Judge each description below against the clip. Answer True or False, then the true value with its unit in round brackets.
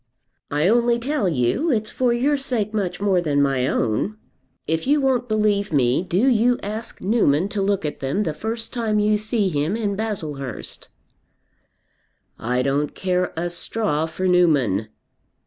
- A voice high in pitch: True (195 Hz)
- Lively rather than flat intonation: True (6.9 semitones)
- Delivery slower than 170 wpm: True (160 wpm)